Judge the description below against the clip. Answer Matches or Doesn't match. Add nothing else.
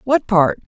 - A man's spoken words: Doesn't match